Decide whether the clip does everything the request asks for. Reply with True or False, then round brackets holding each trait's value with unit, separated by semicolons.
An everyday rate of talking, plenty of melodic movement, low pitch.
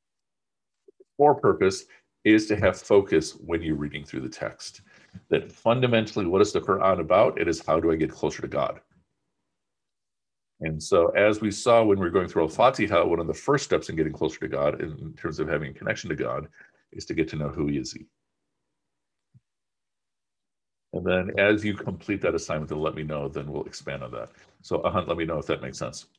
False (210 wpm; 6.5 semitones; 100 Hz)